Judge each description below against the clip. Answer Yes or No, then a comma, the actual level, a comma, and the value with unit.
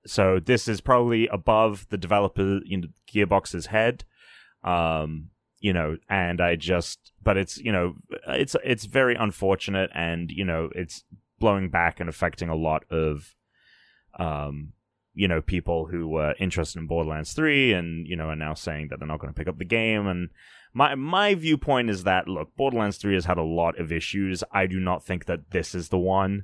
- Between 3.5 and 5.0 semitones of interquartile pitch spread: Yes, average, 4.0 semitones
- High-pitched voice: No, very low, 95 Hz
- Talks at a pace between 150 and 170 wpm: No, average, 195 wpm